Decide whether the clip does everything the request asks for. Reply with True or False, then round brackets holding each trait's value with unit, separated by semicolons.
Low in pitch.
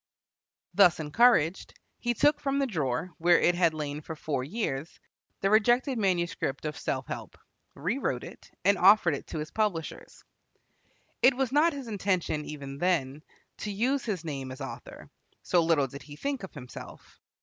False (175 Hz)